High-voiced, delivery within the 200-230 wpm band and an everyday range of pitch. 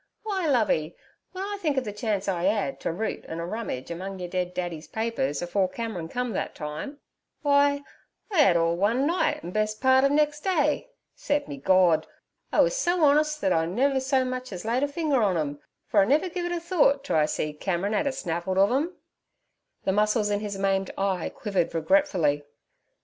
No: high, 215 Hz; fast, 205 wpm; wide, 8.0 semitones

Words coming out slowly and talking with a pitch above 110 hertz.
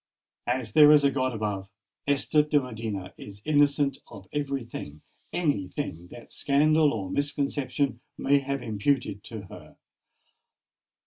Yes: slow, 130 wpm; low, 135 Hz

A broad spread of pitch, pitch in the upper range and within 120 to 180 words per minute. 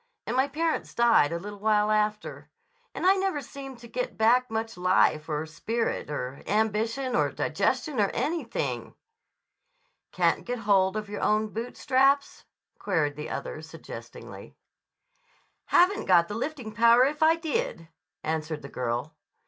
Yes: wide, 6.3 semitones; high, 220 Hz; average, 150 wpm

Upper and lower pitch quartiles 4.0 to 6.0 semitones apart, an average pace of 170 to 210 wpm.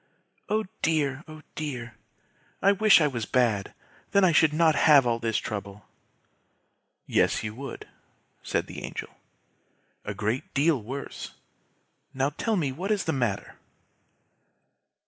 No: wide, 5.5 semitones; slow, 135 wpm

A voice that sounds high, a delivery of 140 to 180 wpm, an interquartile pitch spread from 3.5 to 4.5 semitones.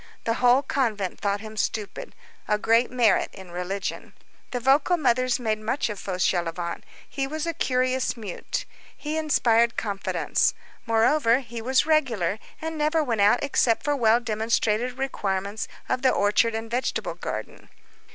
Yes: high, 230 Hz; average, 150 wpm; average, 3.9 semitones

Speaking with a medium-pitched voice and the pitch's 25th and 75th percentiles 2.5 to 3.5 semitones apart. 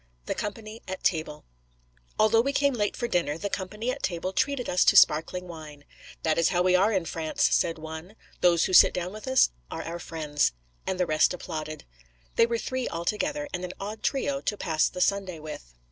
No: medium, 180 Hz; average, 5.0 semitones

